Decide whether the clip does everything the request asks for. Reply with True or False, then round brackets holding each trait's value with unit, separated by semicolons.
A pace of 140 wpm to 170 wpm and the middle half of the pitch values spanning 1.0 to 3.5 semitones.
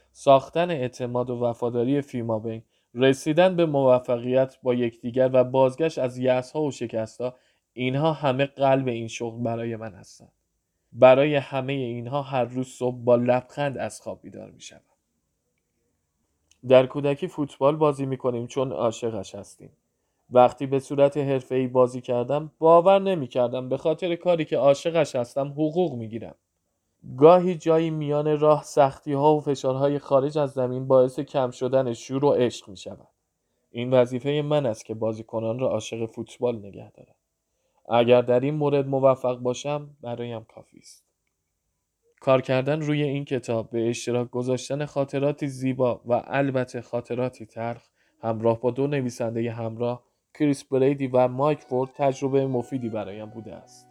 True (150 wpm; 2.9 semitones)